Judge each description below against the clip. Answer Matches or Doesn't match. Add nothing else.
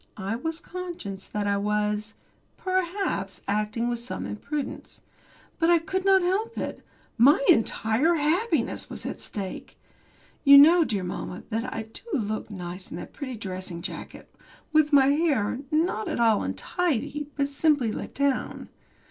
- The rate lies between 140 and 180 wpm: Matches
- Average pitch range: Doesn't match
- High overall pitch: Matches